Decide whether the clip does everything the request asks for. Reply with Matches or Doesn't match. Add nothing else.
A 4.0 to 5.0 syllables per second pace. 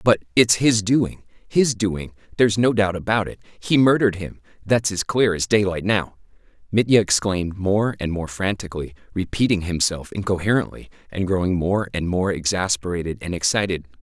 Doesn't match